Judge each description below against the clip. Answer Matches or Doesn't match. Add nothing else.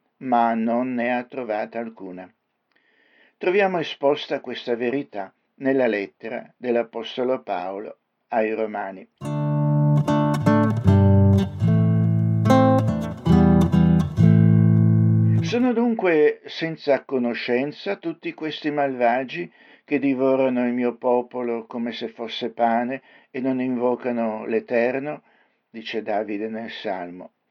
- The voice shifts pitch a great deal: Doesn't match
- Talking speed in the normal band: Doesn't match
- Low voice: Matches